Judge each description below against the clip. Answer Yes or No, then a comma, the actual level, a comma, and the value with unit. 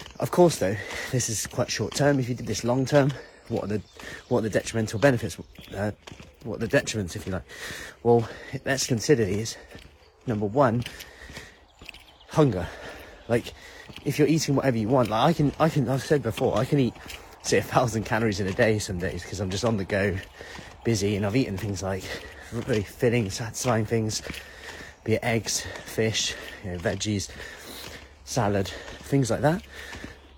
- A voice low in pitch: Yes, low, 110 Hz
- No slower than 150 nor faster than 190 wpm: Yes, average, 175 wpm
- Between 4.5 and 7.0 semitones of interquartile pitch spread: Yes, average, 4.8 semitones